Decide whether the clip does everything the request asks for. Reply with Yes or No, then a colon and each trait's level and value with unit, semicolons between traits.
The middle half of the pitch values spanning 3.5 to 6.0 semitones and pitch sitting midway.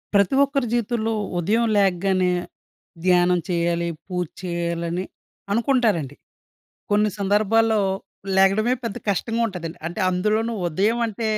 No: average, 4.0 semitones; high, 200 Hz